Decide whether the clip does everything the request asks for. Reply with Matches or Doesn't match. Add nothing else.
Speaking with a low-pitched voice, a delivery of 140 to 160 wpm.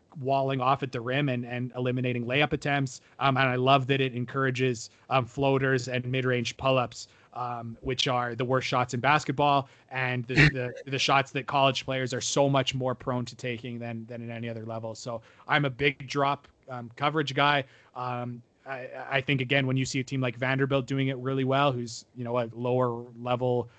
Doesn't match